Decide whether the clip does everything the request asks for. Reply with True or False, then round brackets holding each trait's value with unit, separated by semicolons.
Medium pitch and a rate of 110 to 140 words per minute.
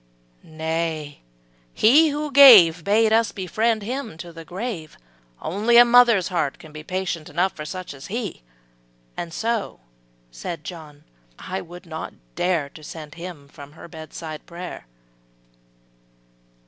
True (175 Hz; 135 wpm)